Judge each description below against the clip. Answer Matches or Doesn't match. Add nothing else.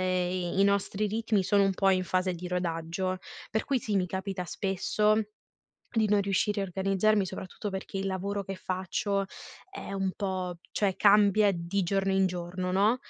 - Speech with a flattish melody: Matches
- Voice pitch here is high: Matches